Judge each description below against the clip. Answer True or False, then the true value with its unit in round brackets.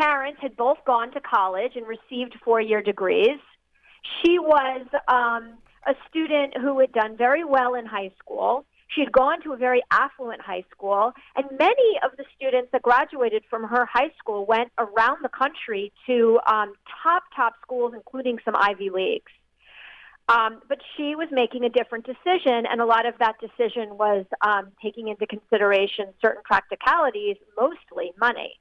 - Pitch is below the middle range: False (245 Hz)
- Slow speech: False (170 wpm)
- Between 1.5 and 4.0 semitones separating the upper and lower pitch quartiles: True (3.7 semitones)